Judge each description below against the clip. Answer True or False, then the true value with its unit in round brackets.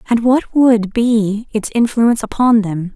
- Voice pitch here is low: False (225 Hz)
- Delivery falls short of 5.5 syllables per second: True (4.1 syllables/s)